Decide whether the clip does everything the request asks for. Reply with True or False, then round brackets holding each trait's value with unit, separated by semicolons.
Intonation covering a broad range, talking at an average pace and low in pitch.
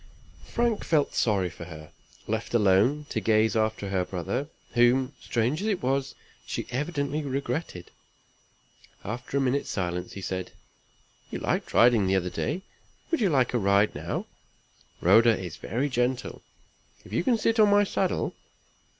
True (6.6 semitones; 155 wpm; 120 Hz)